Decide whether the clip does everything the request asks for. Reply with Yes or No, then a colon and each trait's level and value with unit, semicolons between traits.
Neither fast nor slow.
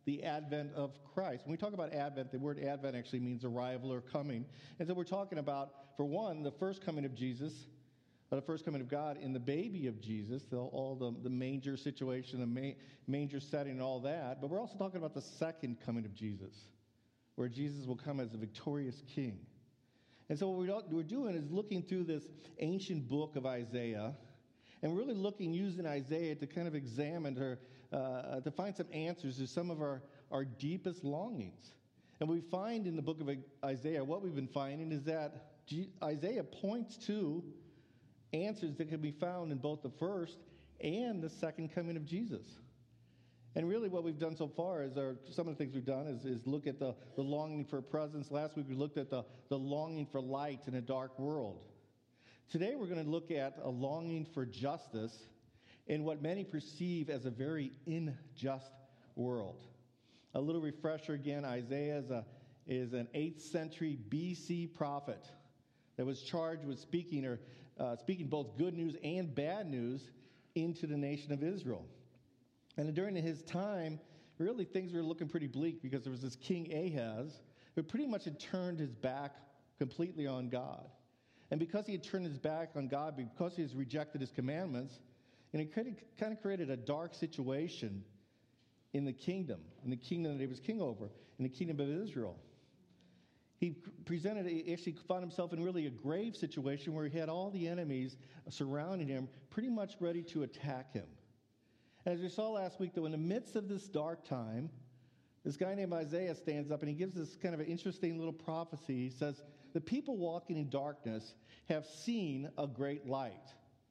Yes: average, 190 wpm